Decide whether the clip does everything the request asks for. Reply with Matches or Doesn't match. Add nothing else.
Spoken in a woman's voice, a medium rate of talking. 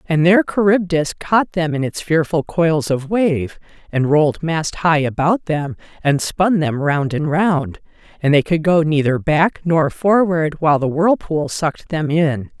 Matches